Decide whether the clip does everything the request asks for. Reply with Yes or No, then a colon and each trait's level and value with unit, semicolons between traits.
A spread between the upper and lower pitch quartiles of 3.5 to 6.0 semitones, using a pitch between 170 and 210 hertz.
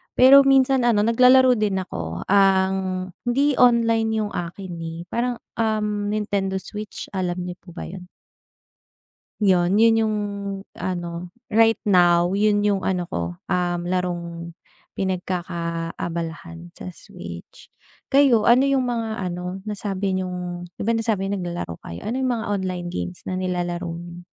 Yes: average, 4.0 semitones; high, 190 Hz